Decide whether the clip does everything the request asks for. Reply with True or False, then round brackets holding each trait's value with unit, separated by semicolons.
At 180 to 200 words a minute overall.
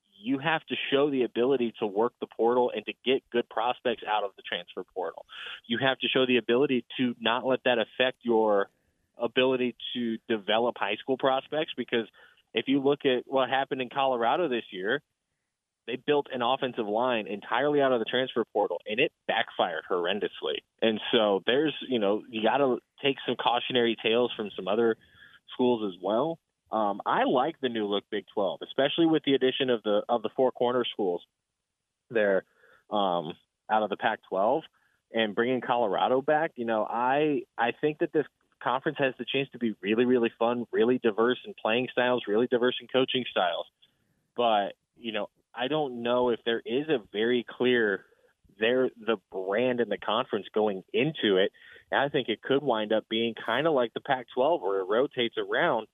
True (190 wpm)